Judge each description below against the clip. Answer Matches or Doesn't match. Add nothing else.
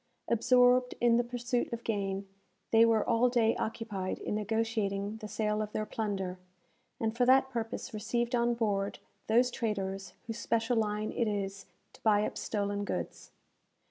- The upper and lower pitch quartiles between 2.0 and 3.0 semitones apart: Matches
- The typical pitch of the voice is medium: Doesn't match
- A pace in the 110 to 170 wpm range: Matches